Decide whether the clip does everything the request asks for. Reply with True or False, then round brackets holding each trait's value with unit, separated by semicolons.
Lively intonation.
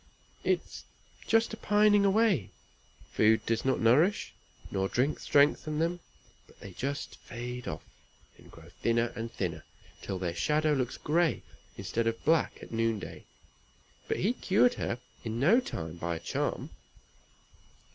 True (7.5 semitones)